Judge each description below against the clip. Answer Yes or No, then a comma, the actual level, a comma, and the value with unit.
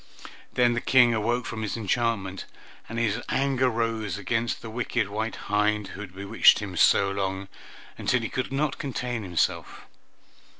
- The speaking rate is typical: Yes, average, 160 wpm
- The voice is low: Yes, low, 115 Hz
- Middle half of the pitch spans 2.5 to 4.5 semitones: Yes, average, 3.0 semitones